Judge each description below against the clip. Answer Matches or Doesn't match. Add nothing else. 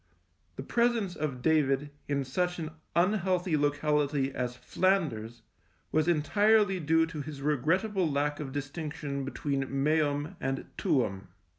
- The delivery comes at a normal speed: Doesn't match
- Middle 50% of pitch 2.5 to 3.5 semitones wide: Doesn't match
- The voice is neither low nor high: Matches